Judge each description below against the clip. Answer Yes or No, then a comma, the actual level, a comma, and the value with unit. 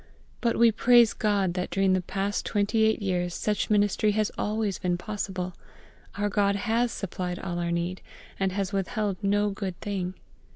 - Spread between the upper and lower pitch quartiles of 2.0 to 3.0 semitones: Yes, narrow, 2.4 semitones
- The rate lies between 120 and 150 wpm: No, average, 170 wpm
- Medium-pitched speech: No, high, 200 Hz